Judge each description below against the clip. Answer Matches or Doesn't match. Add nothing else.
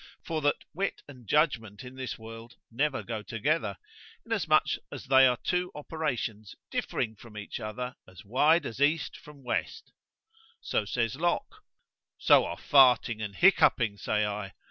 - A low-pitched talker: Matches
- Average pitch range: Doesn't match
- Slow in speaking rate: Doesn't match